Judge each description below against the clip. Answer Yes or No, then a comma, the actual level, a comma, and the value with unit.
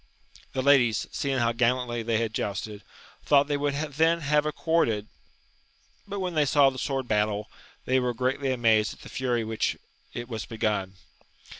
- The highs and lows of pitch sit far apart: No, average, 4.2 semitones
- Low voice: Yes, low, 125 Hz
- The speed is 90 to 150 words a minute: No, average, 170 wpm